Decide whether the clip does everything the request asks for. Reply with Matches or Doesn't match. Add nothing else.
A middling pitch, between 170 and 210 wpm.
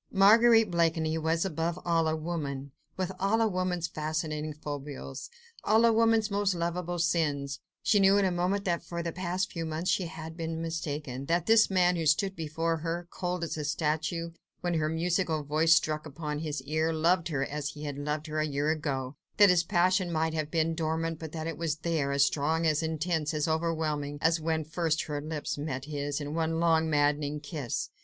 Matches